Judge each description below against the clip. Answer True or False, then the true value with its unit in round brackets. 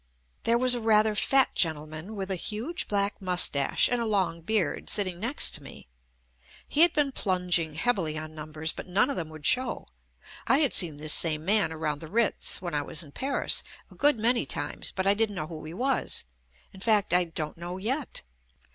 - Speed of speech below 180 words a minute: False (205 wpm)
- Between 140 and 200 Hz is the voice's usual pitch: True (190 Hz)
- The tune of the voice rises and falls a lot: True (6.3 semitones)